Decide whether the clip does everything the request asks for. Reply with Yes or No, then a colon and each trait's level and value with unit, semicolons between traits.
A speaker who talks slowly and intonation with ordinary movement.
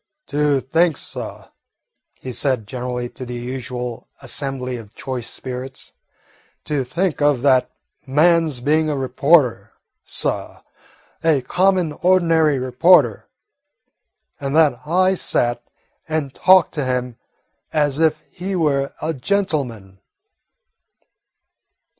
Yes: slow, 110 wpm; average, 4.2 semitones